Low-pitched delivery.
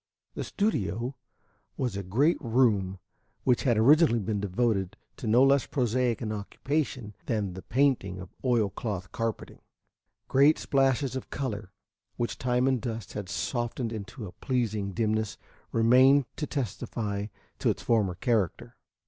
Yes: low, 115 Hz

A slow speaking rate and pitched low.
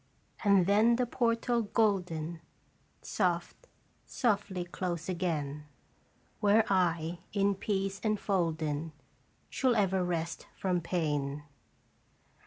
No: slow, 100 wpm; medium, 185 Hz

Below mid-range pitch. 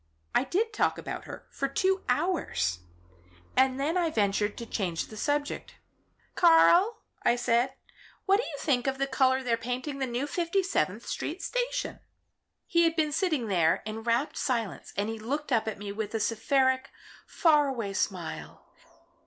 No: very high, 260 Hz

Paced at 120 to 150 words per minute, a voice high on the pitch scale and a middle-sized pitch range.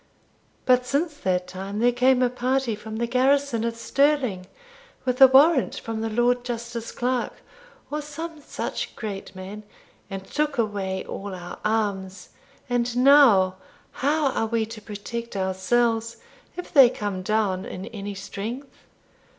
Yes: average, 145 wpm; high, 230 Hz; average, 4.2 semitones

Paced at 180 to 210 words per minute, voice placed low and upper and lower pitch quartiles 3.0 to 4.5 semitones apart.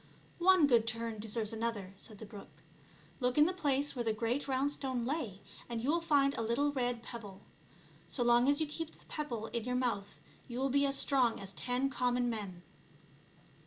No: fast, 205 wpm; high, 245 Hz; average, 3.8 semitones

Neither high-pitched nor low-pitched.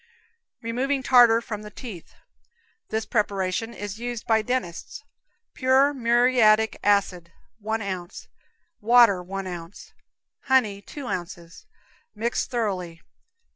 No: high, 220 Hz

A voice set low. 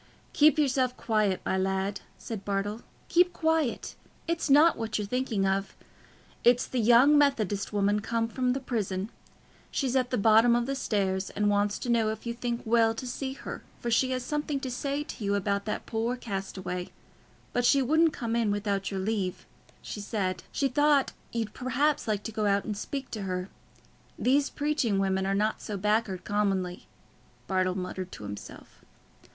No: high, 225 Hz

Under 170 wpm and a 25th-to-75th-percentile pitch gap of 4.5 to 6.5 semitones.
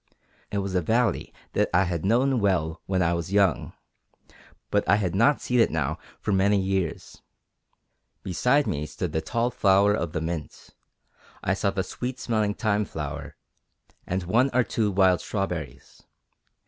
No: average, 160 wpm; average, 4.0 semitones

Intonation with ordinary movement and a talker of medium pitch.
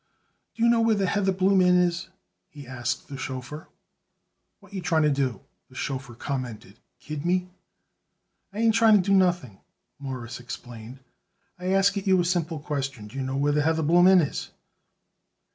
No: wide, 6.1 semitones; medium, 155 Hz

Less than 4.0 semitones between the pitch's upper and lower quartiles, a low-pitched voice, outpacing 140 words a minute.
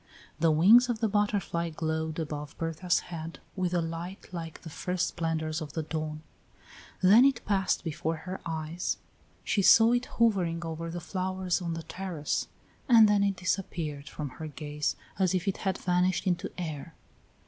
No: average, 3.0 semitones; medium, 170 Hz; average, 170 wpm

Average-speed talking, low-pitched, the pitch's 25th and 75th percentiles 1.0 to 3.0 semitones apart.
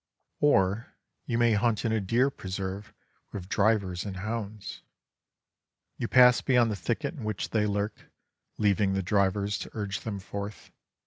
Yes: average, 150 wpm; low, 105 Hz; average, 2.7 semitones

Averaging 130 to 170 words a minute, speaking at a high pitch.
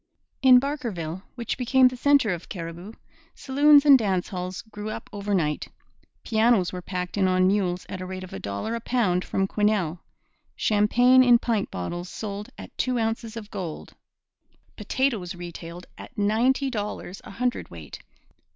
Yes: average, 155 wpm; high, 205 Hz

